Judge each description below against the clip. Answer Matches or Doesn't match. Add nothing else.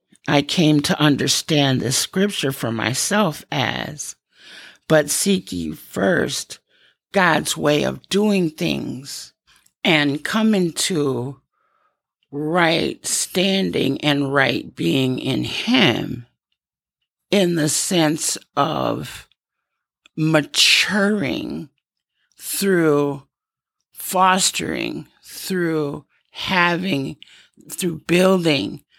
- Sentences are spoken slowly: Matches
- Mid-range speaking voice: Matches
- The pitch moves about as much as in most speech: Matches